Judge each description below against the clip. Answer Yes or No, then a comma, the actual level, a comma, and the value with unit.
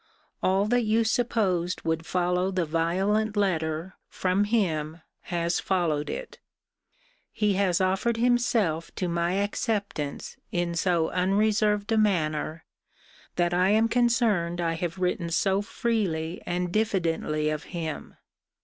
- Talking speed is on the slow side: Yes, slow, 125 wpm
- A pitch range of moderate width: Yes, average, 3.9 semitones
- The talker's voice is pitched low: No, medium, 185 Hz